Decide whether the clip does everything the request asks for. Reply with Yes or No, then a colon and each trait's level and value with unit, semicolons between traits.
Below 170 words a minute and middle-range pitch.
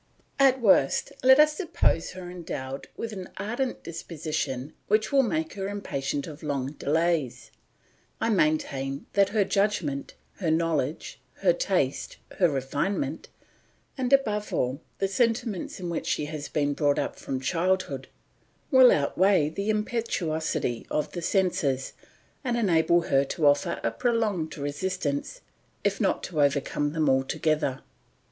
Yes: average, 140 wpm; medium, 165 Hz